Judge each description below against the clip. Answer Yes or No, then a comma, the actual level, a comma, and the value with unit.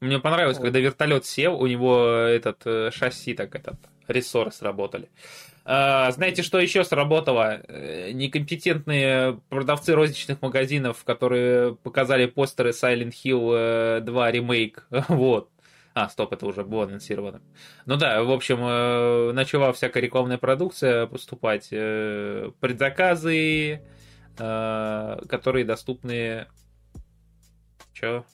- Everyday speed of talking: No, slow, 105 wpm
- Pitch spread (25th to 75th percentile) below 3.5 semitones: Yes, average, 2.9 semitones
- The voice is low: Yes, low, 125 Hz